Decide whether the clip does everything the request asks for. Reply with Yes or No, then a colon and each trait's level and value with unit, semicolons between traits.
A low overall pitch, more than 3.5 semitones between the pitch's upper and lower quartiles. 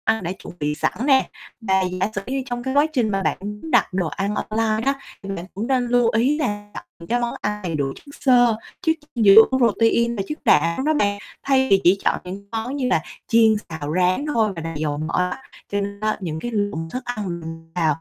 No: high, 210 Hz; average, 5.1 semitones